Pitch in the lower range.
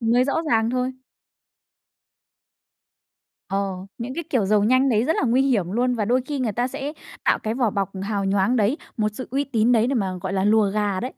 No: high, 230 Hz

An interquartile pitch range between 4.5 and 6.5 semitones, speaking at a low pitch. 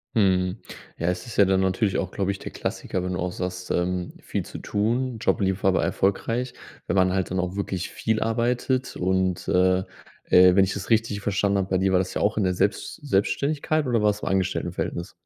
No: average, 2.7 semitones; very low, 95 Hz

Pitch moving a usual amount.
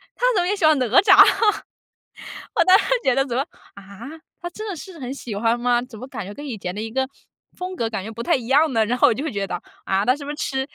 No: wide, 5.7 semitones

